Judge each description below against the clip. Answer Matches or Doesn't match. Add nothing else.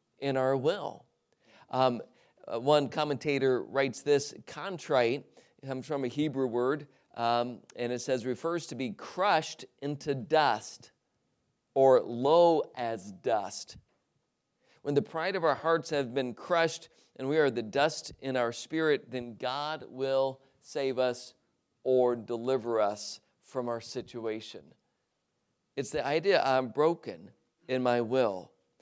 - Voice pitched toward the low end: Matches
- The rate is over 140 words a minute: Doesn't match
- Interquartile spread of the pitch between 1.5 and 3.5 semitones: Matches